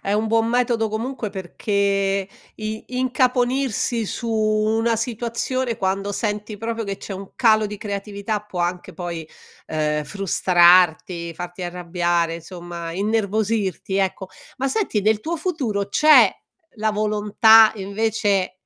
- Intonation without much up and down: No, average, 3.1 semitones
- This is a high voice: Yes, high, 210 Hz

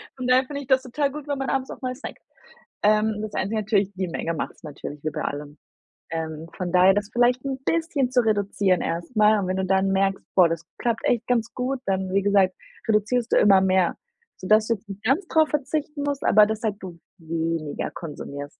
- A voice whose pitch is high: Yes, high, 210 Hz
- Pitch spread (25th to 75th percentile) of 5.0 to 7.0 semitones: Yes, wide, 5.4 semitones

